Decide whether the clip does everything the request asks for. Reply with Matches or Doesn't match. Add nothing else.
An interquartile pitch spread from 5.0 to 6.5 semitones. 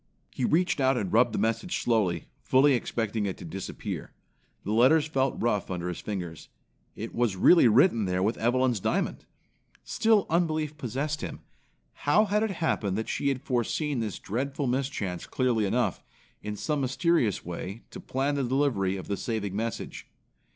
Matches